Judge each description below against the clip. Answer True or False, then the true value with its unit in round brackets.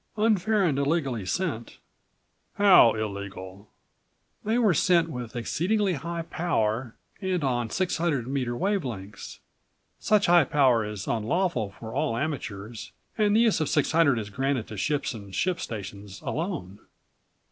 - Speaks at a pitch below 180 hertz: True (135 Hz)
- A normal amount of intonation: False (8.2 semitones)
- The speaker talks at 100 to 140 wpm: True (135 wpm)